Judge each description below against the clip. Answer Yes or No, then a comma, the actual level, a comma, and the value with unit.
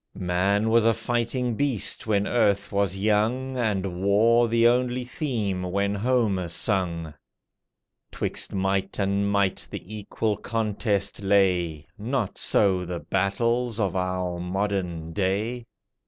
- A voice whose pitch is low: Yes, low, 100 Hz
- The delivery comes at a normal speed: No, slow, 125 wpm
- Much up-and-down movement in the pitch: No, average, 3.6 semitones